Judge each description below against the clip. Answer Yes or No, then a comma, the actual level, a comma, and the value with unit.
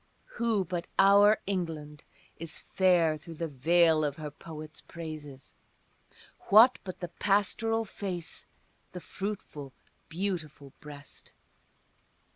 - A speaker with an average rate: No, slow, 105 wpm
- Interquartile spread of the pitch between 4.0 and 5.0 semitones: Yes, average, 4.3 semitones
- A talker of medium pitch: Yes, medium, 170 Hz